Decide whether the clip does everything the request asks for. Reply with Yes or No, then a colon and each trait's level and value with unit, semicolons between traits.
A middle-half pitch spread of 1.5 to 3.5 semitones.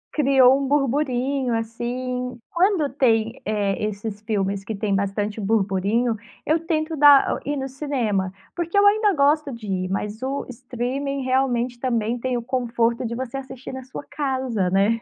No: average, 3.9 semitones